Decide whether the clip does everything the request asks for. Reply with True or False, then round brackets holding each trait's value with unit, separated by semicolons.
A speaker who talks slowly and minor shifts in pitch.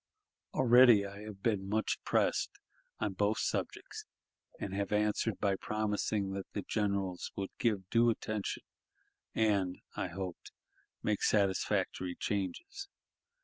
True (120 wpm; 2.0 semitones)